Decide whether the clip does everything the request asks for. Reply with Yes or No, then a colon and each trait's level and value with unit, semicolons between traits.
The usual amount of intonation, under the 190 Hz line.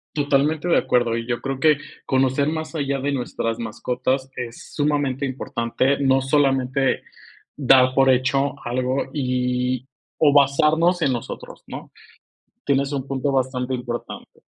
No: narrow, 2.0 semitones; low, 135 Hz